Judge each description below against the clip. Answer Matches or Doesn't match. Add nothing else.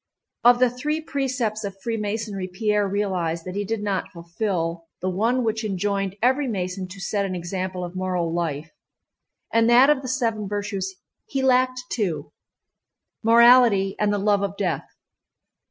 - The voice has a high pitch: Matches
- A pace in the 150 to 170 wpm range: Matches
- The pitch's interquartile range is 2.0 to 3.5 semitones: Doesn't match